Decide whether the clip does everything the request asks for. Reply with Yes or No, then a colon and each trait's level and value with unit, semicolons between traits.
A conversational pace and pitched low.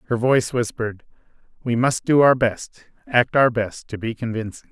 Yes: average, 180 wpm; low, 120 Hz